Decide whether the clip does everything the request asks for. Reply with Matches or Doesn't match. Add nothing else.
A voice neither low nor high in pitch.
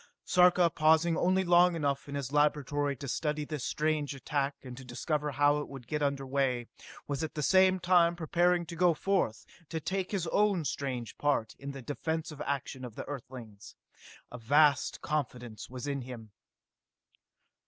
Matches